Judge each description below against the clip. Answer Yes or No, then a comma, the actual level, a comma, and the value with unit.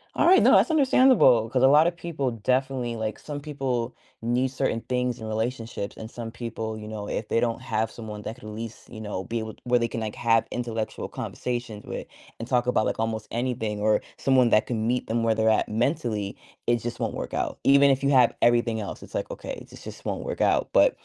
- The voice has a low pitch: Yes, low, 115 Hz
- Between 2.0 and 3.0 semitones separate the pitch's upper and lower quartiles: Yes, narrow, 2.4 semitones